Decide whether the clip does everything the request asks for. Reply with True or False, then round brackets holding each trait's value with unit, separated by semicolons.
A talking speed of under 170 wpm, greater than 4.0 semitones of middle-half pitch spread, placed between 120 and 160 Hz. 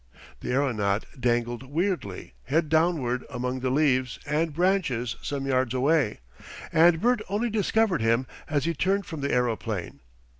True (145 wpm; 5.3 semitones; 135 Hz)